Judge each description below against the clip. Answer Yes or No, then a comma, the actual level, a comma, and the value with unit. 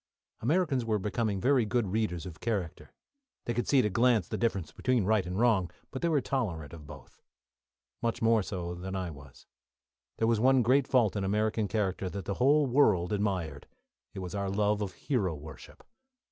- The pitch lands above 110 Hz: No, low, 105 Hz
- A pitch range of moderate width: Yes, average, 4.6 semitones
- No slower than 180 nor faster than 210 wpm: Yes, average, 190 wpm